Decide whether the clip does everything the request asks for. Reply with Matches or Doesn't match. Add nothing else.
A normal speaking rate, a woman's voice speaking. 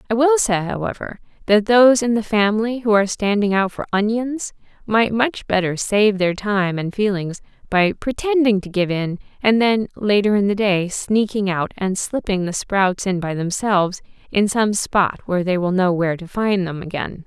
Matches